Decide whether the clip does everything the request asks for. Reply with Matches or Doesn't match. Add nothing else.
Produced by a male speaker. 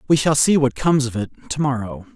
Matches